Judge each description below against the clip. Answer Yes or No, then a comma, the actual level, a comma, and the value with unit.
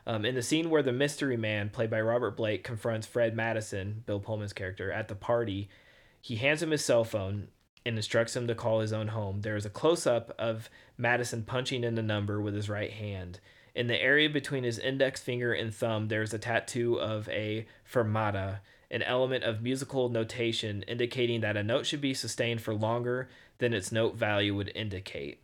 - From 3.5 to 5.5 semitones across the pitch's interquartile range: No, narrow, 2.5 semitones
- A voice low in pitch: Yes, low, 115 Hz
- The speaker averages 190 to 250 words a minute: Yes, average, 200 wpm